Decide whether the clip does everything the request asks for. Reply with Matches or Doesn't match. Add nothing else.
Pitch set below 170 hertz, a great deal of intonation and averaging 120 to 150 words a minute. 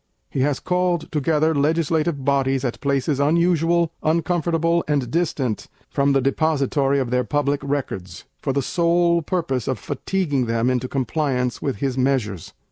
Doesn't match